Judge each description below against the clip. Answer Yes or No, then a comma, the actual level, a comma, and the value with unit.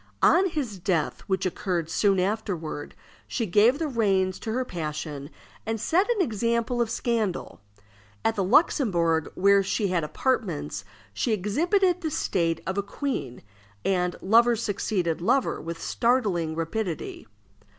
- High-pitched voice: Yes, high, 200 Hz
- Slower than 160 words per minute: Yes, average, 140 wpm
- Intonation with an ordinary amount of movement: No, wide, 5.7 semitones